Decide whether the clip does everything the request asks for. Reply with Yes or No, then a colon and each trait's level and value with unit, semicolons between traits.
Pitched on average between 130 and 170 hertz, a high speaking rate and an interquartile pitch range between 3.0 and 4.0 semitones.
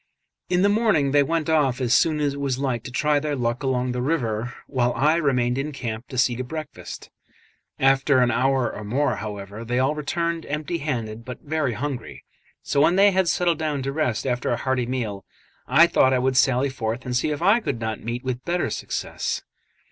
Yes: low, 135 Hz; fast, 210 wpm; average, 3.6 semitones